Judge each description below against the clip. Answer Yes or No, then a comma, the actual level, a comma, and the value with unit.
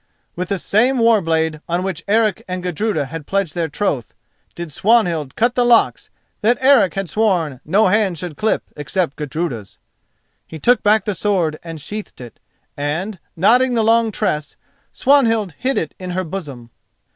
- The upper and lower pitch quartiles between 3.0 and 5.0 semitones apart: No, wide, 5.5 semitones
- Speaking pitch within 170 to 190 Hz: Yes, medium, 185 Hz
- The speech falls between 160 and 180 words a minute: Yes, average, 170 wpm